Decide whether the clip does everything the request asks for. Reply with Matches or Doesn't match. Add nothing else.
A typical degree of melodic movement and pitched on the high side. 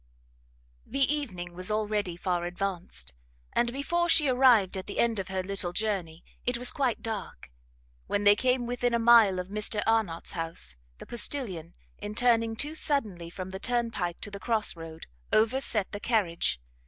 Matches